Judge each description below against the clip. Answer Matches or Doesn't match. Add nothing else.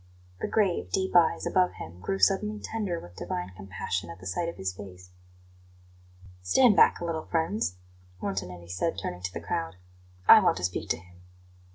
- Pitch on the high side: Doesn't match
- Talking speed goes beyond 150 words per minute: Matches